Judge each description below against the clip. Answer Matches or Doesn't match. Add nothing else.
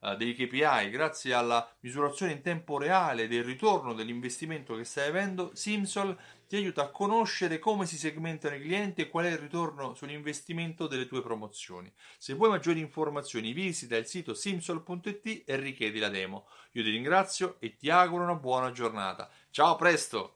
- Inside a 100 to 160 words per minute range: Doesn't match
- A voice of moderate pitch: Matches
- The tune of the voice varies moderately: Doesn't match